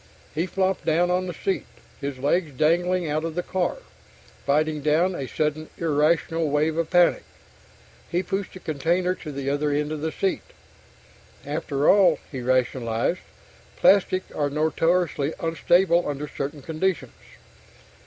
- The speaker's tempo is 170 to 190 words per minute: No, average, 145 wpm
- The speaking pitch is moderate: Yes, medium, 160 Hz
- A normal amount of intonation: Yes, average, 3.3 semitones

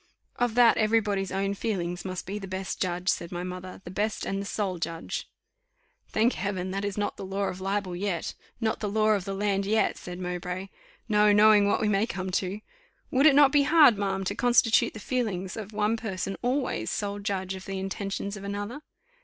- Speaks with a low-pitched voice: No, high, 200 Hz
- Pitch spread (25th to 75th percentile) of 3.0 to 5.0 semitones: No, narrow, 2.5 semitones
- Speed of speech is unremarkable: No, fast, 210 wpm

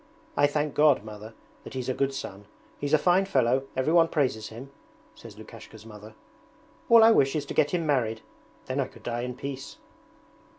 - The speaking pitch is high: No, low, 135 Hz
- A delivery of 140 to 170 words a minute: No, average, 185 wpm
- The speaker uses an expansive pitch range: No, average, 4.5 semitones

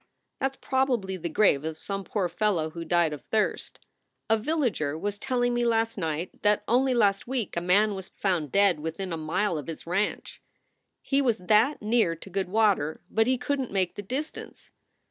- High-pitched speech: Yes, high, 200 Hz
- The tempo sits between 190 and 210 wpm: Yes, average, 195 wpm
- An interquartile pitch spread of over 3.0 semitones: Yes, wide, 5.4 semitones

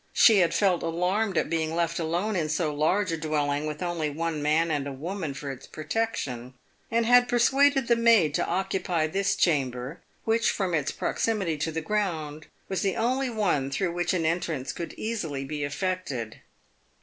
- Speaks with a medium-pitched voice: Yes, medium, 165 Hz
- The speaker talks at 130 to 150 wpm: No, average, 180 wpm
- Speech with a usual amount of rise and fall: Yes, average, 4.8 semitones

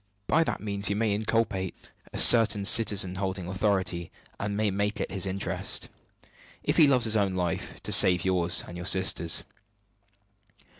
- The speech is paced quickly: No, average, 160 wpm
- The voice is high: No, low, 100 Hz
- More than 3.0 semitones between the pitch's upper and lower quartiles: No, narrow, 2.5 semitones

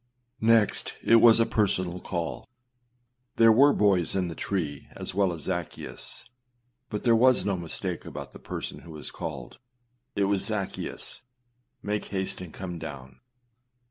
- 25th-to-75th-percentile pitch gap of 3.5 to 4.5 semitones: Yes, average, 4.1 semitones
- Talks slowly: No, average, 160 wpm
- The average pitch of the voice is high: No, very low, 95 Hz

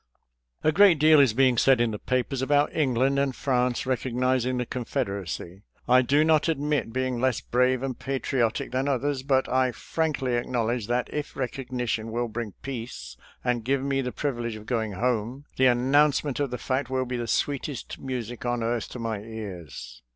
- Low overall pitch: Yes, low, 125 Hz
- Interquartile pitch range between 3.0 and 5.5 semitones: No, narrow, 2.4 semitones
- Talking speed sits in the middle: Yes, average, 195 wpm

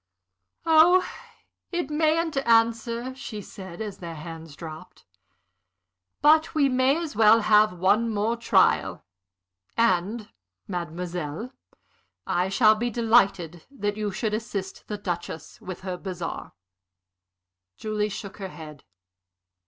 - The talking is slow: Yes, slow, 115 wpm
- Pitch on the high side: Yes, high, 210 Hz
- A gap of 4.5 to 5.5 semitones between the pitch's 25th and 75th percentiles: Yes, average, 4.8 semitones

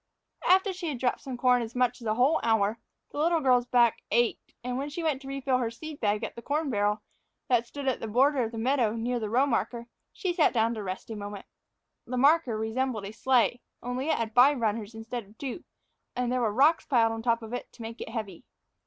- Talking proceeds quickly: Yes, fast, 235 wpm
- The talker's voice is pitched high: Yes, high, 245 Hz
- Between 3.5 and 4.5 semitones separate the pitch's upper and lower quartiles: No, average, 3.1 semitones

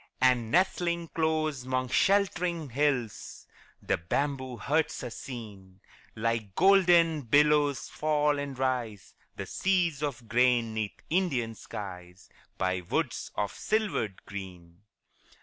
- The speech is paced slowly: Yes, slow, 115 wpm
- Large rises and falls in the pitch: Yes, wide, 6.2 semitones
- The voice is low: Yes, low, 130 Hz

